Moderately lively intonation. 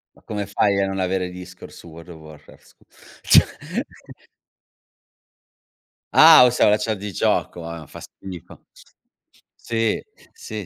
Yes: average, 3.5 semitones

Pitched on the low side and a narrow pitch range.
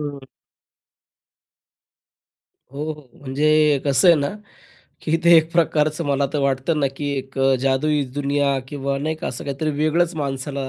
No: medium, 145 Hz; narrow, 2.0 semitones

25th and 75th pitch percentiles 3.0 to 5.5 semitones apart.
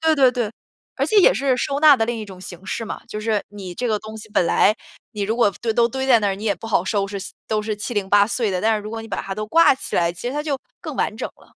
Yes: average, 3.3 semitones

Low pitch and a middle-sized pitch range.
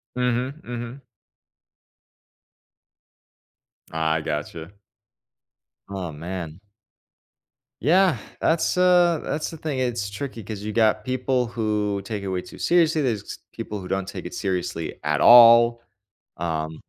No: low, 110 Hz; wide, 5.8 semitones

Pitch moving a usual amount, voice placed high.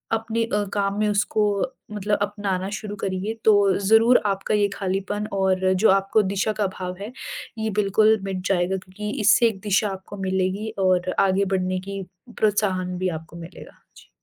No: narrow, 2.0 semitones; high, 195 Hz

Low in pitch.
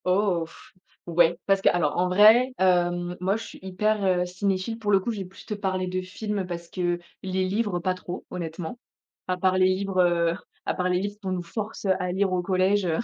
No: medium, 185 Hz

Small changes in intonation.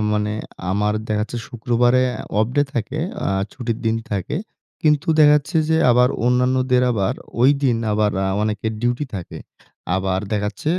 No: average, 3.5 semitones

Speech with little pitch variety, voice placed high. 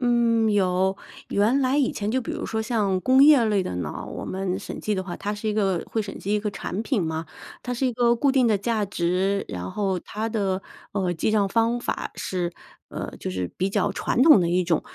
No: average, 3.7 semitones; high, 205 Hz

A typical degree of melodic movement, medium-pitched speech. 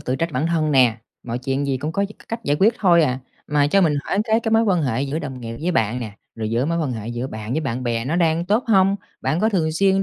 No: wide, 6.4 semitones; medium, 150 Hz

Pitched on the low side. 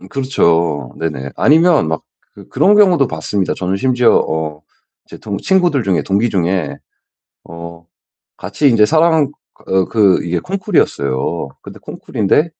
Yes: very low, 95 Hz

